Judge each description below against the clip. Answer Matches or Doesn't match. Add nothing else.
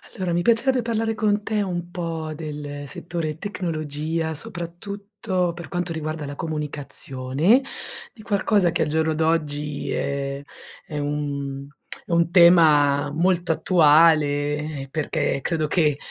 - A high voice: Doesn't match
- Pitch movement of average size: Matches